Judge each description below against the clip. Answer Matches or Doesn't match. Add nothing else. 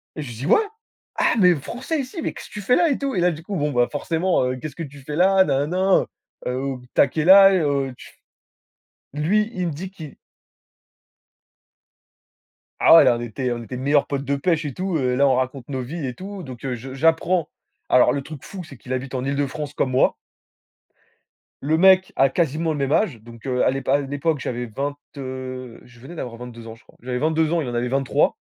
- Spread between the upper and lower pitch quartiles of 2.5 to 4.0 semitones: Doesn't match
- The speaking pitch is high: Doesn't match